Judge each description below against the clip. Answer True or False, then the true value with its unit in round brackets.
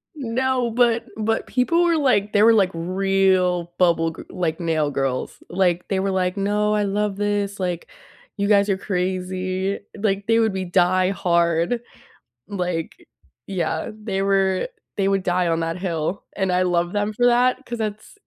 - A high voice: True (195 Hz)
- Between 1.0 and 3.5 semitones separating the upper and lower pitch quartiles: True (2.8 semitones)